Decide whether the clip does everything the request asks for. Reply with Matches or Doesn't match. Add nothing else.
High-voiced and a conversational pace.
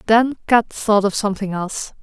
Matches